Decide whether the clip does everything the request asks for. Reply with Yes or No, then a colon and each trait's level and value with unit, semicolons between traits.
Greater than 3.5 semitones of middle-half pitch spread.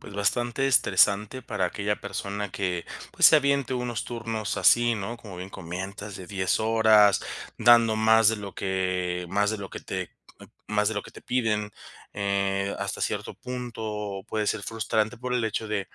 No: narrow, 2.4 semitones